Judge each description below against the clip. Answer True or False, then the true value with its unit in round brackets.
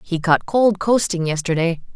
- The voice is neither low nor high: True (180 Hz)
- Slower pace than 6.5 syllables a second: True (4.6 syllables/s)